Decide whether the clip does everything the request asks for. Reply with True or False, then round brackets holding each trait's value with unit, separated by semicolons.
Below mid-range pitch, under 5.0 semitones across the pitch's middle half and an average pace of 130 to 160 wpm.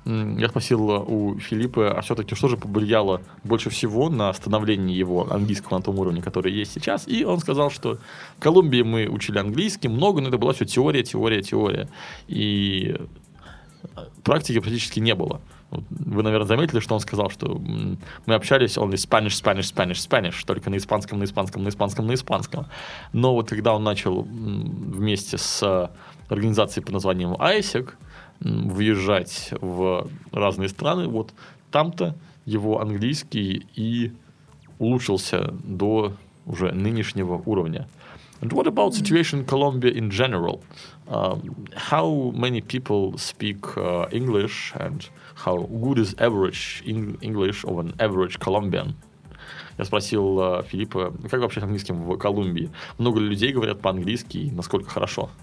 True (105 Hz; 3.2 semitones; 145 wpm)